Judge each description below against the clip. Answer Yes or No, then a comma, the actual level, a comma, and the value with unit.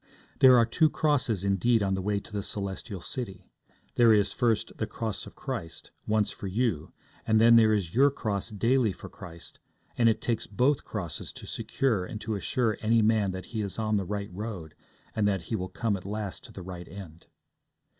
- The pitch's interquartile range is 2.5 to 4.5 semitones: Yes, average, 3.1 semitones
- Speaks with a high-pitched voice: No, low, 105 Hz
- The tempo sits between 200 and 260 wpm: Yes, fast, 205 wpm